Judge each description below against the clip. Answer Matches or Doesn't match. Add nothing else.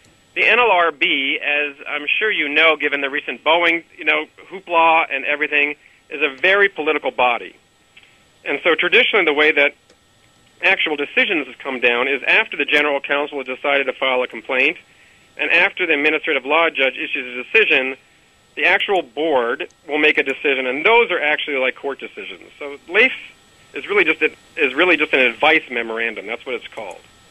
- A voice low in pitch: Doesn't match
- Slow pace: Doesn't match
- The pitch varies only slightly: Matches